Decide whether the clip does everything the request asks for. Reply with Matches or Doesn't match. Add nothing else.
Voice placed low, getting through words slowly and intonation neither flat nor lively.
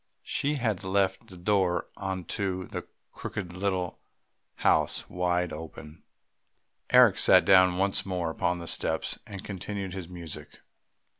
Doesn't match